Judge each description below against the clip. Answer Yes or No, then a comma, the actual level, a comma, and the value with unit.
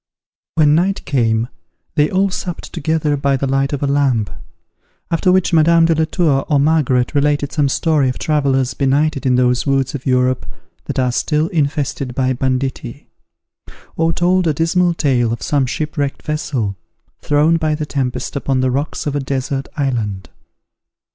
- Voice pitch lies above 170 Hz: No, medium, 140 Hz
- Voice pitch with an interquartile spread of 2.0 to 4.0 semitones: Yes, average, 3.1 semitones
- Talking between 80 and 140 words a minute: No, average, 165 wpm